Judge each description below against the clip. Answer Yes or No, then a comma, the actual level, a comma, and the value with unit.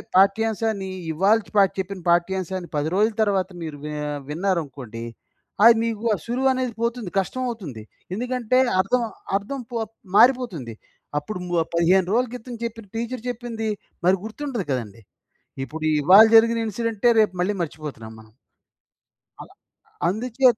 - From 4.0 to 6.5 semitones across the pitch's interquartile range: Yes, average, 5.3 semitones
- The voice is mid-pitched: No, high, 205 Hz